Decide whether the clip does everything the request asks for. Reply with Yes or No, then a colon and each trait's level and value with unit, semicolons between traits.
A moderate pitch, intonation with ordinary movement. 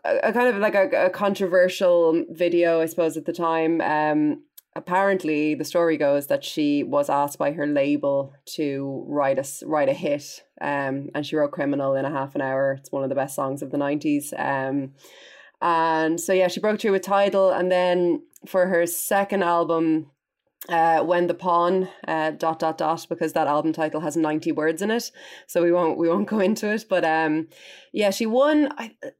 Yes: medium, 165 Hz; average, 4.3 semitones